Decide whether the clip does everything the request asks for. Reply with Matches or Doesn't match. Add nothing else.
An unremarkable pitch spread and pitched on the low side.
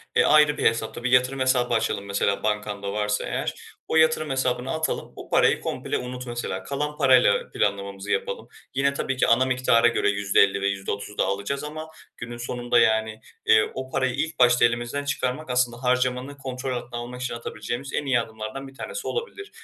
Matches